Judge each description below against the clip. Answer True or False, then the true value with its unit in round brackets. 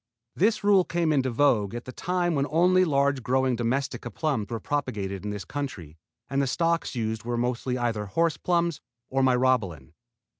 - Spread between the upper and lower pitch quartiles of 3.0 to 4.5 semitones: False (5.4 semitones)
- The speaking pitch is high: False (130 Hz)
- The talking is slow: False (175 wpm)